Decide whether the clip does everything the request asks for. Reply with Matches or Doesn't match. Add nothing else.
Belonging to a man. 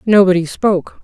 Doesn't match